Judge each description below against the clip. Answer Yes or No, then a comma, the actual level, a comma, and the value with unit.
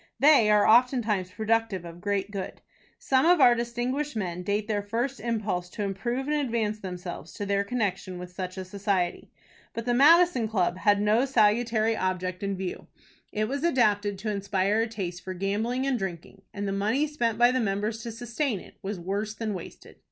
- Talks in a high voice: Yes, high, 210 Hz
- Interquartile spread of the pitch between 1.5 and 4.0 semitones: Yes, average, 3.7 semitones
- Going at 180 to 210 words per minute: Yes, average, 190 wpm